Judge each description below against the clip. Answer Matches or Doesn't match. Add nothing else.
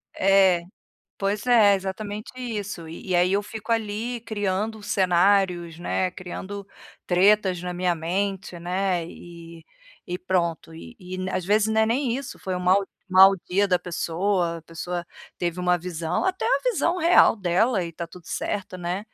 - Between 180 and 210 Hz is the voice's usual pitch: Matches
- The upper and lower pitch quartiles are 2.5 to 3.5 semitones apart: Matches